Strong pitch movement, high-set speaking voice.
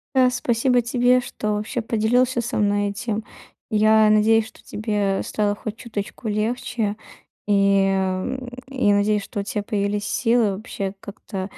No: narrow, 2.6 semitones; high, 215 Hz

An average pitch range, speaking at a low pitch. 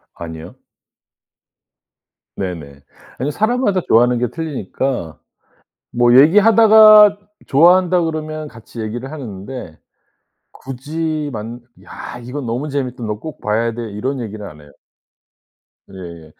No: wide, 6.6 semitones; low, 125 Hz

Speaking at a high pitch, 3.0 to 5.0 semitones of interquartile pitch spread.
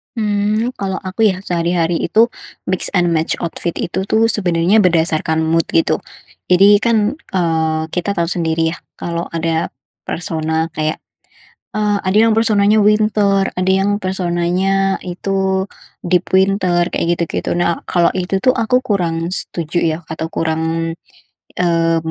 No: medium, 180 Hz; average, 3.4 semitones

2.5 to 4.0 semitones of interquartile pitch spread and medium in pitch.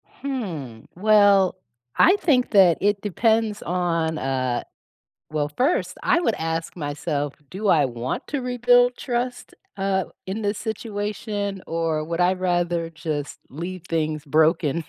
No: average, 5.2 semitones; medium, 180 Hz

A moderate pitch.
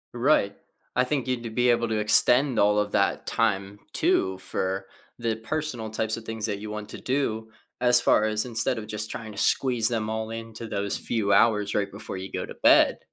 No: low, 110 Hz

